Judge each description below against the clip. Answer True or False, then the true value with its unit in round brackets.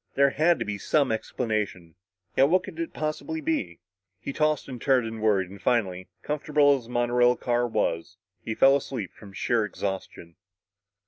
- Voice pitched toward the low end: True (120 Hz)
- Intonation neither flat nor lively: False (5.8 semitones)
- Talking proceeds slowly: False (175 wpm)